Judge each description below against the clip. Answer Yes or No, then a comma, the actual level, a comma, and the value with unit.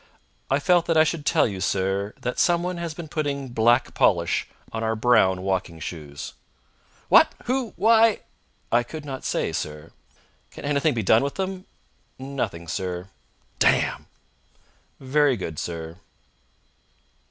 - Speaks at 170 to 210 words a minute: No, average, 140 wpm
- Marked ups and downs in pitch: Yes, wide, 8.8 semitones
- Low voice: Yes, low, 120 Hz